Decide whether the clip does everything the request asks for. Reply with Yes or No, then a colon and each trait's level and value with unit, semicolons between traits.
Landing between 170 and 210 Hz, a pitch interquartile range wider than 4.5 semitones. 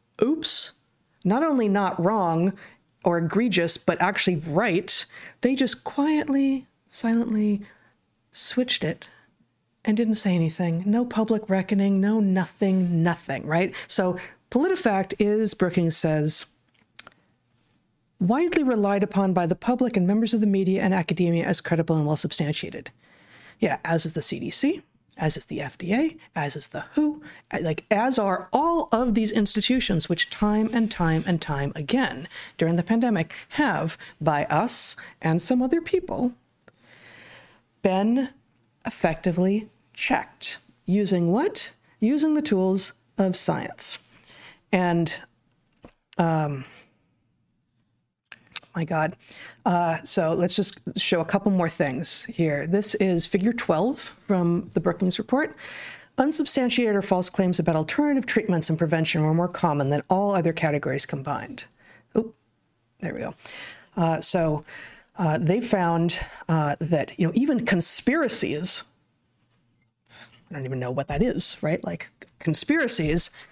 Yes: high, 190 Hz; average, 5.1 semitones